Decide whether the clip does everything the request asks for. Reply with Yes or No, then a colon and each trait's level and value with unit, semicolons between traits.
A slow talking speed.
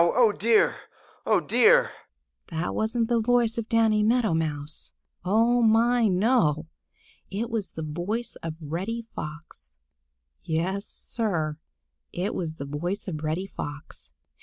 Yes: slow, 130 wpm